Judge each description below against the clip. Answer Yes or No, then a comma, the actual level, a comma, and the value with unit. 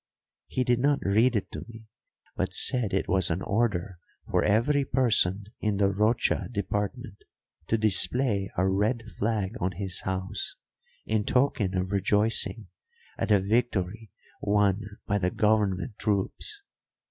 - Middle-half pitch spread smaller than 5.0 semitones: Yes, average, 3.2 semitones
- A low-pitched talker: Yes, low, 105 Hz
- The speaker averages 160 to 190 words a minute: No, average, 140 wpm